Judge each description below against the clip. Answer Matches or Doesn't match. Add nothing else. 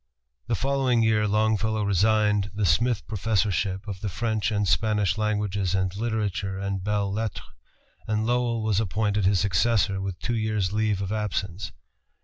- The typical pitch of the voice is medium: Doesn't match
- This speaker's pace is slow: Doesn't match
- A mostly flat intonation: Matches